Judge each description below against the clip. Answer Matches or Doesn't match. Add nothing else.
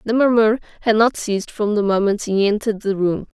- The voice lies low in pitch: Doesn't match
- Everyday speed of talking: Doesn't match